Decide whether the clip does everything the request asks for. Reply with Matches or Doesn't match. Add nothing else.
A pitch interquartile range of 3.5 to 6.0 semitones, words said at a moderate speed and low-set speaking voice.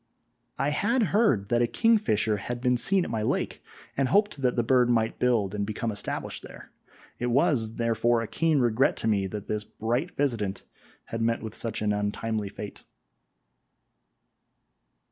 Matches